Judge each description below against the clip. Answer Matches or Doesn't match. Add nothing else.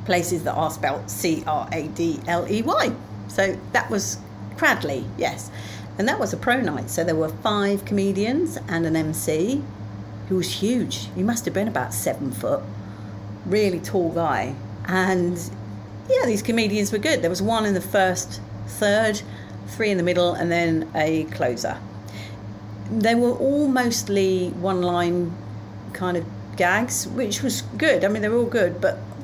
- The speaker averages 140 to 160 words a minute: Doesn't match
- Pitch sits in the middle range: Matches